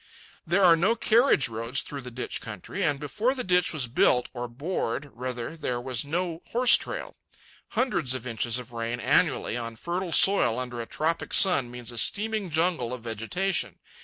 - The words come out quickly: No, average, 180 wpm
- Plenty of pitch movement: Yes, wide, 7.0 semitones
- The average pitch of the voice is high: No, low, 135 Hz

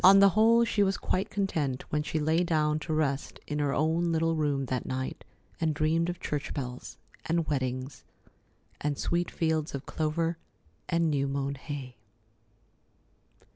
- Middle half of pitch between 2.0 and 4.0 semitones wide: Yes, average, 3.1 semitones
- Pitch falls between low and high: Yes, medium, 155 Hz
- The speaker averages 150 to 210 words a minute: Yes, average, 160 wpm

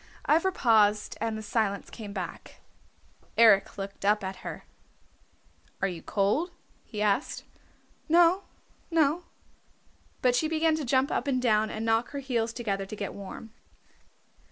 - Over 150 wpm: No, average, 145 wpm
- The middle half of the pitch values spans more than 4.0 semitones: Yes, wide, 5.5 semitones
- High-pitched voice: Yes, high, 225 Hz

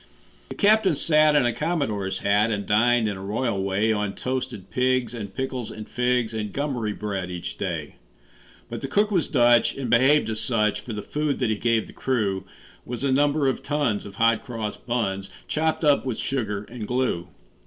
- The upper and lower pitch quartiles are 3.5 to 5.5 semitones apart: Yes, average, 4.2 semitones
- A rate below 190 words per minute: No, average, 195 wpm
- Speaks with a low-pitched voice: Yes, low, 120 Hz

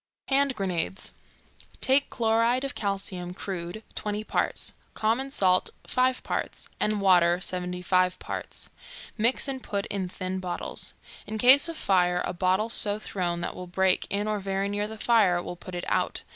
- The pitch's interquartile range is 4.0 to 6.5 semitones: No, average, 3.6 semitones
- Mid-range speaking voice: No, high, 200 Hz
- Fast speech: No, average, 165 wpm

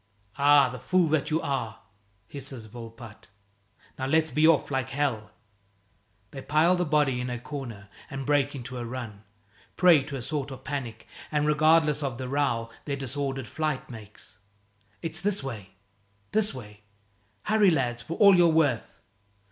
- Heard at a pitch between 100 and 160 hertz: Yes, low, 135 Hz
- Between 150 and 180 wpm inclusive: Yes, average, 160 wpm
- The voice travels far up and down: No, average, 4.0 semitones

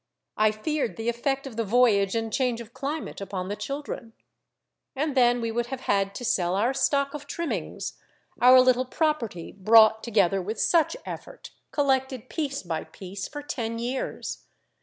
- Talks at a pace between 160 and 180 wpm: Yes, average, 165 wpm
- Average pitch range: Yes, average, 4.2 semitones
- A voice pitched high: Yes, high, 240 Hz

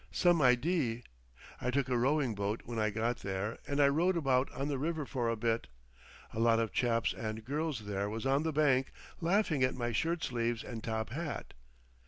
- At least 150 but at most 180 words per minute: No, average, 200 wpm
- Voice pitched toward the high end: No, low, 125 Hz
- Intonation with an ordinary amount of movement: Yes, average, 4.5 semitones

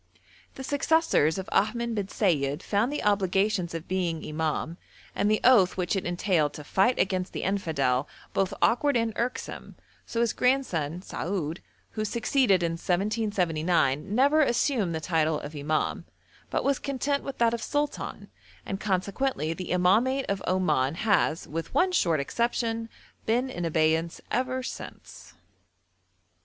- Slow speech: No, average, 145 wpm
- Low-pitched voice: No, high, 190 Hz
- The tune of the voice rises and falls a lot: Yes, wide, 6.3 semitones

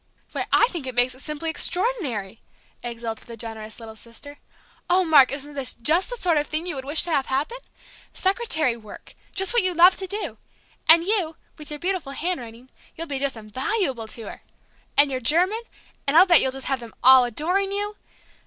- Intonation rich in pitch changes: Yes, wide, 6.5 semitones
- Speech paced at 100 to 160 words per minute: No, average, 200 wpm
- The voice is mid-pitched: No, very high, 290 Hz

